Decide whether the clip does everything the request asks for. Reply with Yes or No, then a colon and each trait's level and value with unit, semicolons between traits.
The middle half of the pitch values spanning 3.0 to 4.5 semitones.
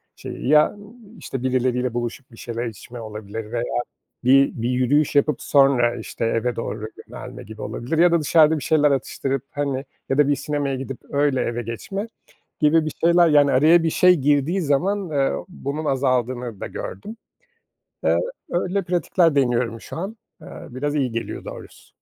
Yes: average, 4.2 semitones